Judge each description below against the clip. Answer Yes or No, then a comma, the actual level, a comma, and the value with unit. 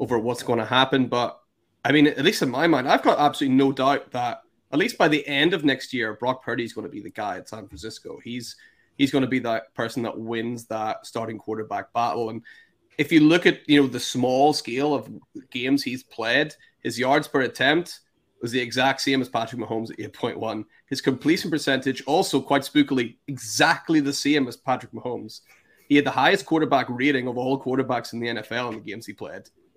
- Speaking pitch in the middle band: No, low, 125 Hz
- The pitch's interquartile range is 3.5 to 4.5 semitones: No, average, 3.1 semitones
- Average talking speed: No, fast, 215 wpm